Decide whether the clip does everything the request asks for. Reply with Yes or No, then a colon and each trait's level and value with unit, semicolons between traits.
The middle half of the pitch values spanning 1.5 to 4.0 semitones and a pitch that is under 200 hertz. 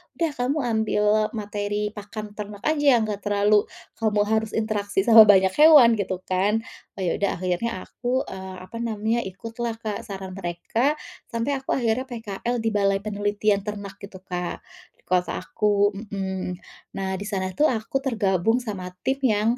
No: average, 2.8 semitones; high, 210 Hz